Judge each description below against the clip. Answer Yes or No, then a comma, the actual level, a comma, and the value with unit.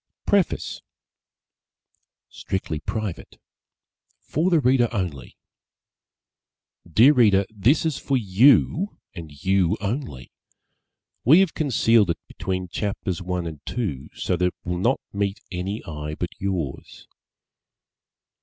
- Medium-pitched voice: No, low, 100 Hz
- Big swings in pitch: Yes, wide, 6.0 semitones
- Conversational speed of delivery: No, slow, 115 wpm